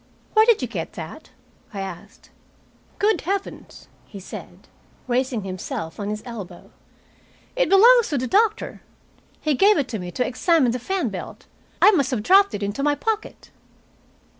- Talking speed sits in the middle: Yes, average, 165 wpm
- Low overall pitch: No, very high, 265 Hz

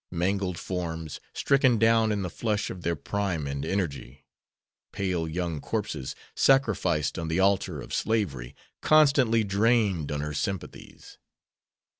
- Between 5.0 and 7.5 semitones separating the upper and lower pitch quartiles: Yes, average, 5.3 semitones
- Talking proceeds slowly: Yes, slow, 130 wpm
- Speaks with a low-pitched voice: Yes, very low, 95 Hz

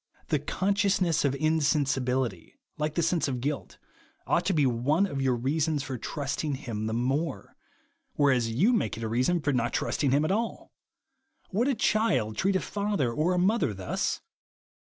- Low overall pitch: No, medium, 145 Hz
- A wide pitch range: Yes, wide, 6.0 semitones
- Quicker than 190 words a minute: No, average, 170 wpm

